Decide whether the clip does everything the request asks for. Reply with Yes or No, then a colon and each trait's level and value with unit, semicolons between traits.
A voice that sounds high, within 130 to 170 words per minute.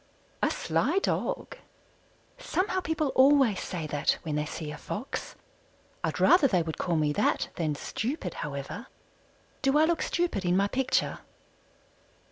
Yes: high, 200 Hz; average, 145 wpm